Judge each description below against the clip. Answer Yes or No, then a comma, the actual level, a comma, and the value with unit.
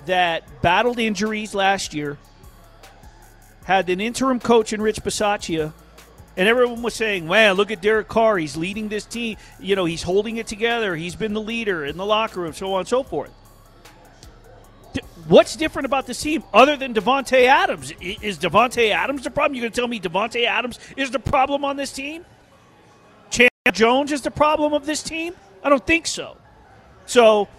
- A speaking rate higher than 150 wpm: Yes, average, 185 wpm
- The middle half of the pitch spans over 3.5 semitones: Yes, average, 5.2 semitones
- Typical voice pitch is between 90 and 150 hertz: No, high, 220 Hz